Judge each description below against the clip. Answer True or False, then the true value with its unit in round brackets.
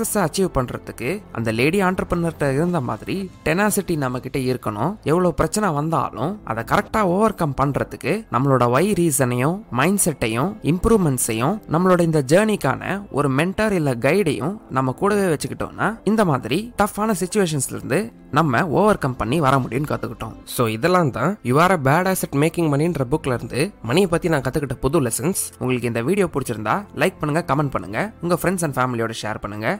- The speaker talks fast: True (150 wpm)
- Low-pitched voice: False (160 Hz)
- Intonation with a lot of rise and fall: True (6.2 semitones)